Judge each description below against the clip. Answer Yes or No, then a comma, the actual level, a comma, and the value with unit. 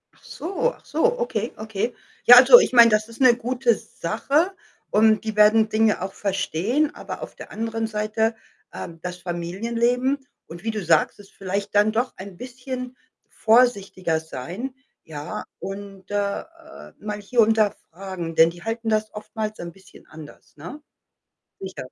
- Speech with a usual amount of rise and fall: Yes, average, 3.9 semitones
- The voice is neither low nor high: No, high, 215 Hz